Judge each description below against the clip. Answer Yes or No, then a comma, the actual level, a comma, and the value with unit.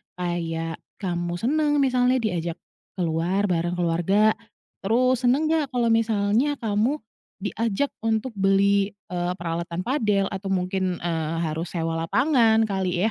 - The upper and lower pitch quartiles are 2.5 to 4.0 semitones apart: No, average, 4.8 semitones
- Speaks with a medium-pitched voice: No, high, 195 Hz